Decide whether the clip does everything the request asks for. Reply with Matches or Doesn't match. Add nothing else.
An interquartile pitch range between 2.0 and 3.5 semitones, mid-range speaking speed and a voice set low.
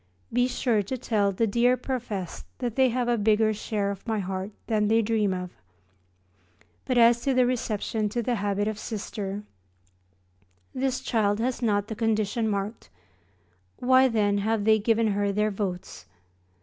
Doesn't match